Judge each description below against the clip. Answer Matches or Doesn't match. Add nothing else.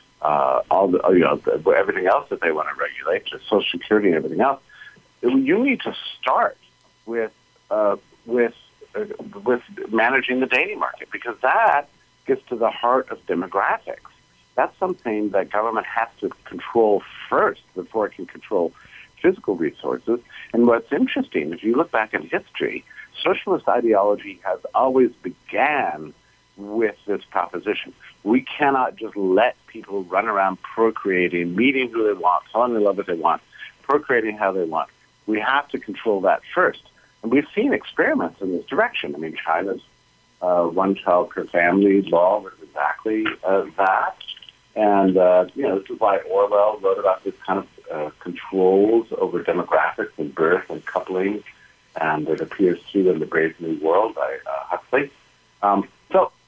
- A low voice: Matches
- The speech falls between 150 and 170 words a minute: Matches